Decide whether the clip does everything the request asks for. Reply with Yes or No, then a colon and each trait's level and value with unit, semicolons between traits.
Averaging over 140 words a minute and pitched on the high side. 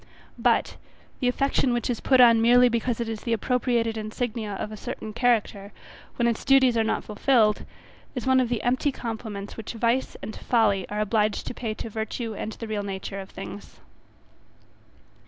Yes: average, 180 wpm; high, 230 Hz